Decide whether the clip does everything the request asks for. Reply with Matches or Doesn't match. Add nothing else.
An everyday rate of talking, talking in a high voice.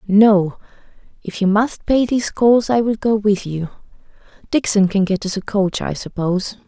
Matches